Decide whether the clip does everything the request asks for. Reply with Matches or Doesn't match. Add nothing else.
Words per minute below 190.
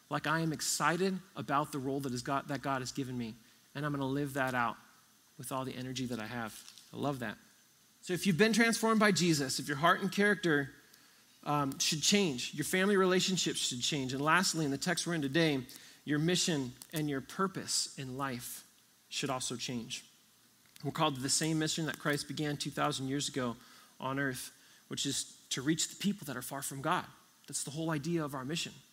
Doesn't match